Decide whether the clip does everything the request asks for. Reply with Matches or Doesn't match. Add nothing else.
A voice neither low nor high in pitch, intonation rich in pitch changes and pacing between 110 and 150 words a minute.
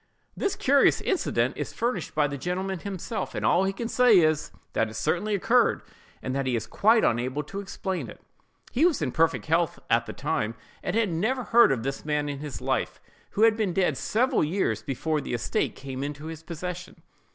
Doesn't match